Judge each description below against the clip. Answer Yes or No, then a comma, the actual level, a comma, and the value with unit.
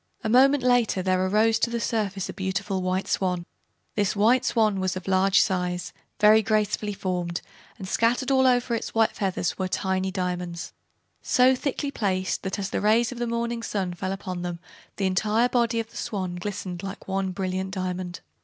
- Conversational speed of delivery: Yes, average, 180 wpm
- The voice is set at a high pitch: Yes, high, 195 Hz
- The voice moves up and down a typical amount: Yes, average, 3.4 semitones